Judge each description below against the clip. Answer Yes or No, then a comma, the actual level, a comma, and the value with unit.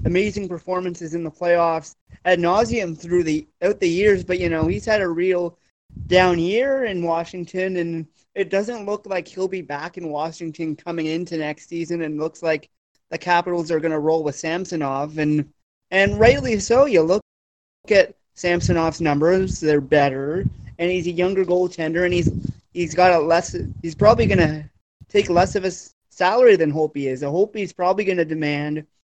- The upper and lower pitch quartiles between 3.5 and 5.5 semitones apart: No, average, 2.8 semitones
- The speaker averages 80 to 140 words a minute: No, average, 190 wpm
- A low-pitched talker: No, medium, 170 Hz